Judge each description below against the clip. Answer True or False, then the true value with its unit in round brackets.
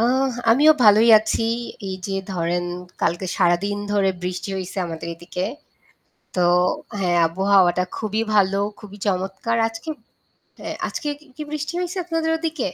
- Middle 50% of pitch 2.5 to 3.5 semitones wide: False (4.1 semitones)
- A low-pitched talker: False (200 Hz)